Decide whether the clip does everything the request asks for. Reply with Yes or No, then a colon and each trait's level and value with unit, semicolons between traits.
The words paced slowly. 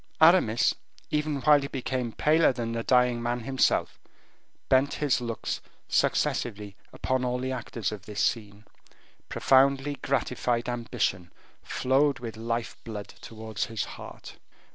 Yes: slow, 130 wpm